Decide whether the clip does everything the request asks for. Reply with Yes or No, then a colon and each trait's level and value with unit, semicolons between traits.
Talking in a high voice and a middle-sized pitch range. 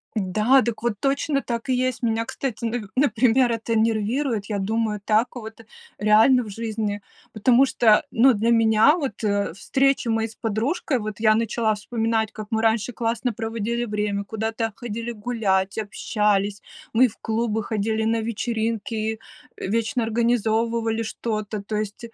No: high, 225 Hz; narrow, 1.7 semitones